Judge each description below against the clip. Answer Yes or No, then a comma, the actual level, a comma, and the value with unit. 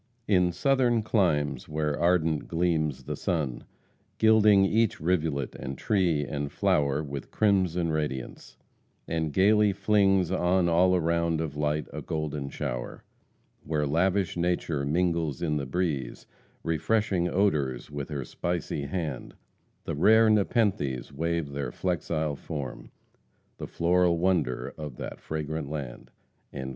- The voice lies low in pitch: Yes, very low, 80 Hz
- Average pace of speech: No, slow, 125 wpm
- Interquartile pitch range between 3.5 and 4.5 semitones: Yes, average, 4.0 semitones